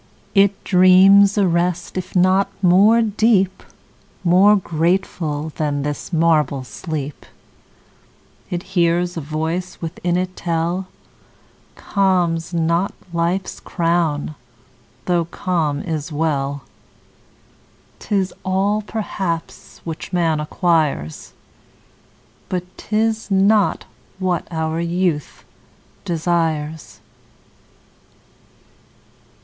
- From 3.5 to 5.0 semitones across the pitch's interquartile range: No, average, 2.9 semitones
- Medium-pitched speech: Yes, medium, 175 Hz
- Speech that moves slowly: Yes, slow, 85 wpm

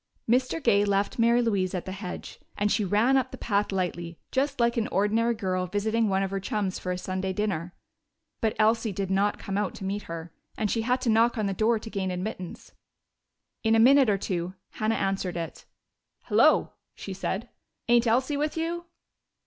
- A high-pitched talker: Yes, high, 205 Hz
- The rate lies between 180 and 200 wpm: Yes, average, 195 wpm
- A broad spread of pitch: No, average, 3.5 semitones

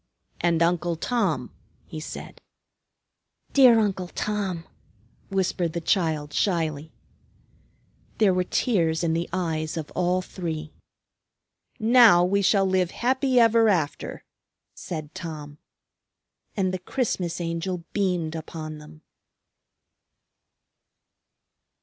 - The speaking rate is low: Yes, slow, 100 wpm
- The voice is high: No, medium, 175 Hz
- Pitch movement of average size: Yes, average, 3.5 semitones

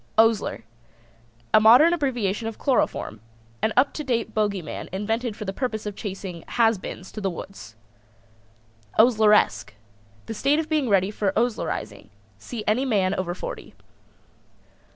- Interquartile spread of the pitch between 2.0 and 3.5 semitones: No, average, 4.0 semitones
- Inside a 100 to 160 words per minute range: Yes, average, 145 wpm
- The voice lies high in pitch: Yes, high, 215 Hz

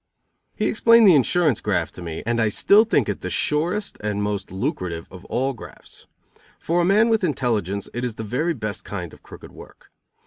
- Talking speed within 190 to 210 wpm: Yes, average, 200 wpm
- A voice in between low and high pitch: No, low, 120 Hz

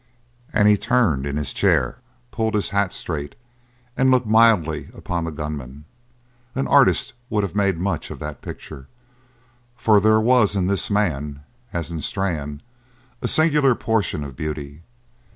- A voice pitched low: Yes, very low, 95 Hz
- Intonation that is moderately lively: No, wide, 6.5 semitones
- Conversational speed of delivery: Yes, average, 150 wpm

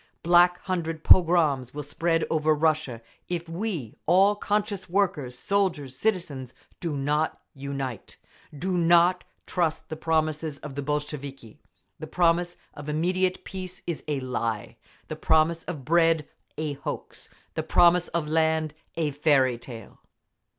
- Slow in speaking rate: Yes, slow, 120 wpm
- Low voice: No, medium, 160 Hz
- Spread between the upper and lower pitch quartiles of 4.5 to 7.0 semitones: No, average, 3.5 semitones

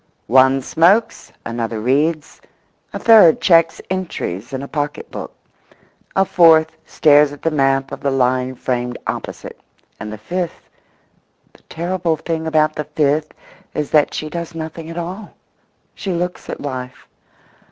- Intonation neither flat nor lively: Yes, average, 3.9 semitones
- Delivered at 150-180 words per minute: No, average, 140 wpm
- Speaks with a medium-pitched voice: Yes, medium, 155 Hz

